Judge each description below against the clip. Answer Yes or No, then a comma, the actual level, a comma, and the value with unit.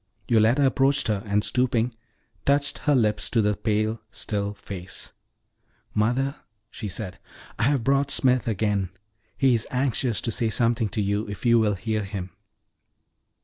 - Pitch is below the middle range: Yes, low, 110 Hz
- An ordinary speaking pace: Yes, average, 150 wpm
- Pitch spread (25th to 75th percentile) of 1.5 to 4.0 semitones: Yes, average, 3.5 semitones